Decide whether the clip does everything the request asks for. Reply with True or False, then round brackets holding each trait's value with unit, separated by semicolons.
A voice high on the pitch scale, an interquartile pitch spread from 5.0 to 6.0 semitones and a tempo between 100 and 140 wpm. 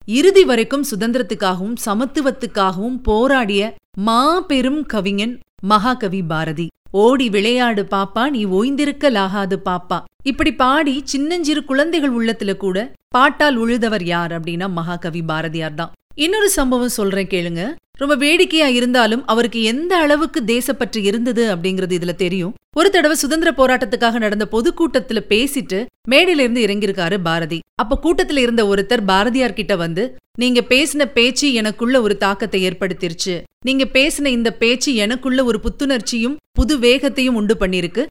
True (235 Hz; 5.4 semitones; 125 wpm)